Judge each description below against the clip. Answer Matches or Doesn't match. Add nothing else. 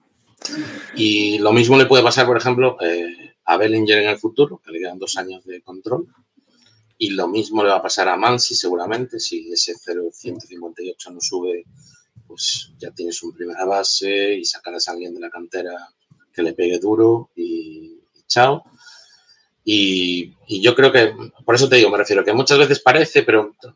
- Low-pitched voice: Matches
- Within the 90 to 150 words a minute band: Doesn't match